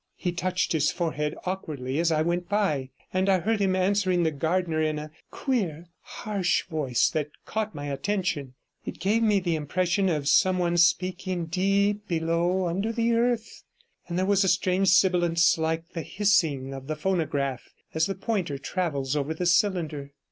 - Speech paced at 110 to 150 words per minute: No, average, 170 wpm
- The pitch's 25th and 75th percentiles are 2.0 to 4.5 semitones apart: Yes, average, 3.6 semitones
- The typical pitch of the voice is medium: Yes, medium, 175 Hz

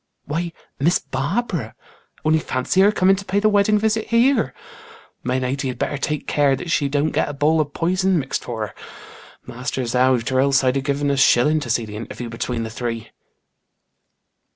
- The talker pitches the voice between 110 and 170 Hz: Yes, medium, 140 Hz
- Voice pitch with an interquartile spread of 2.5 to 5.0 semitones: No, wide, 5.6 semitones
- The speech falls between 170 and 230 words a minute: Yes, average, 190 wpm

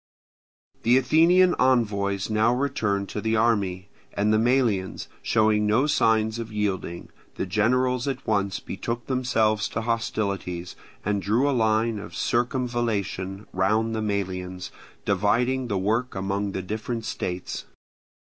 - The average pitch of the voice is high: No, low, 110 Hz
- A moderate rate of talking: No, slow, 130 wpm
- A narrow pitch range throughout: No, average, 3.2 semitones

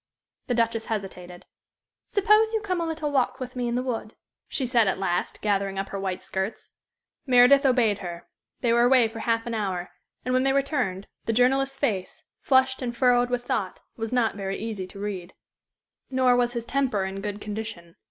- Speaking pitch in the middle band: No, high, 235 Hz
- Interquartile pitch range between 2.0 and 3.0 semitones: No, average, 4.5 semitones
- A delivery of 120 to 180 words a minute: No, average, 190 wpm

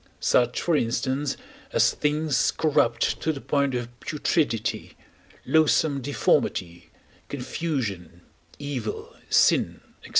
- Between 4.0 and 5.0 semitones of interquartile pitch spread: Yes, average, 4.3 semitones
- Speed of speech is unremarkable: No, slow, 100 wpm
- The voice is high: No, medium, 140 Hz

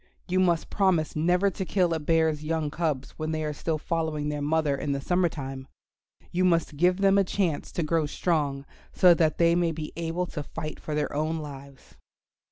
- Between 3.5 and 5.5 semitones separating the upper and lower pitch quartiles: No, narrow, 2.6 semitones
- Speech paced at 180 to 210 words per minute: Yes, average, 200 wpm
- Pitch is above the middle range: No, medium, 160 Hz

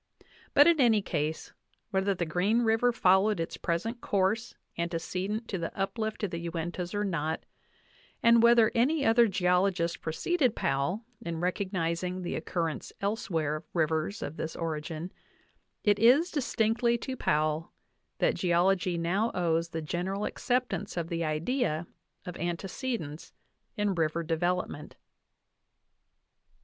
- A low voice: No, medium, 180 Hz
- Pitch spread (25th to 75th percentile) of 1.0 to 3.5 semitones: No, average, 4.9 semitones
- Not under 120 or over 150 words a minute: Yes, slow, 135 wpm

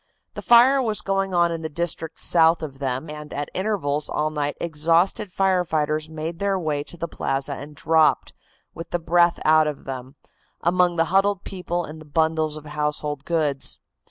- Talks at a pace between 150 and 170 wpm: No, average, 185 wpm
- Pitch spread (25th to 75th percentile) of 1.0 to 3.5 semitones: Yes, average, 2.8 semitones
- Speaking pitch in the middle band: Yes, medium, 160 Hz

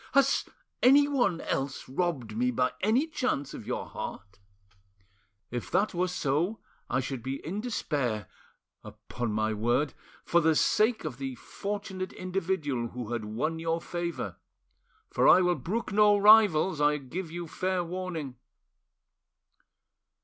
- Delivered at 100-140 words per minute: Yes, slow, 135 wpm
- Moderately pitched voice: Yes, medium, 165 Hz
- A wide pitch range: Yes, wide, 6.7 semitones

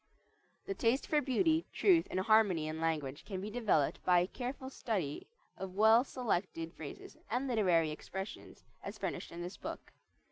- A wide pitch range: Yes, wide, 6.7 semitones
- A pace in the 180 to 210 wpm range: No, average, 155 wpm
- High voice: Yes, high, 200 Hz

